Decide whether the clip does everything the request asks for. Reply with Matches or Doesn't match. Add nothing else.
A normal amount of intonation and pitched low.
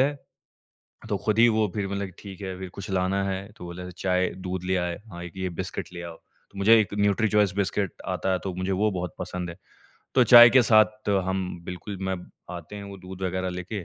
Doesn't match